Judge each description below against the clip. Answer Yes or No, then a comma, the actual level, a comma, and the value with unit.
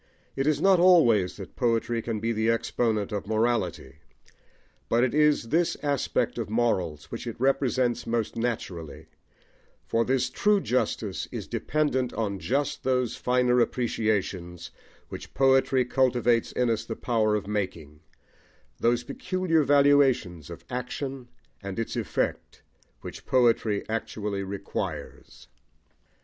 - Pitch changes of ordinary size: Yes, average, 3.9 semitones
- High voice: No, low, 120 Hz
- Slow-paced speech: Yes, slow, 130 wpm